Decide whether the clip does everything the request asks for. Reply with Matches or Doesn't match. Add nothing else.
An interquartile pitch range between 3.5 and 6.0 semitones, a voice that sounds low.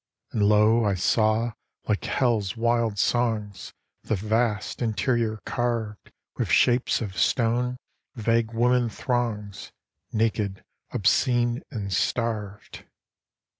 Doesn't match